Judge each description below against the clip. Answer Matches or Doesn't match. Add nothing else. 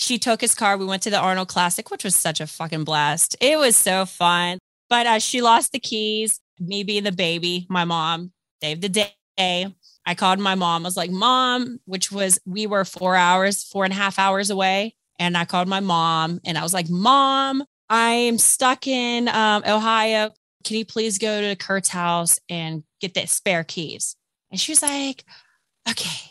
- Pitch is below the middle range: Doesn't match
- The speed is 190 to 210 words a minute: Matches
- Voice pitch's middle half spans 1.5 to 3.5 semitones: Doesn't match